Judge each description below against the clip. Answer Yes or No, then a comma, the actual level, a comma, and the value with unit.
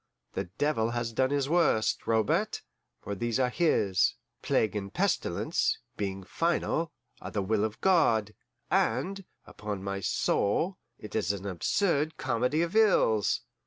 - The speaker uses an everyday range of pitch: No, wide, 7.4 semitones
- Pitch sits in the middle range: No, low, 115 Hz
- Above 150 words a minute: No, average, 140 wpm